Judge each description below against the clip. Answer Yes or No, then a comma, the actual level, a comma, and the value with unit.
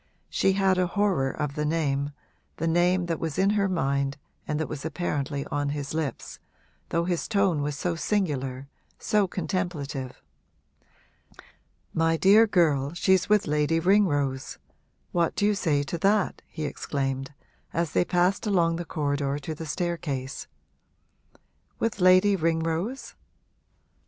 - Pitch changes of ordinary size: Yes, average, 4.4 semitones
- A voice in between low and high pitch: Yes, medium, 165 Hz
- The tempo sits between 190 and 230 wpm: No, average, 140 wpm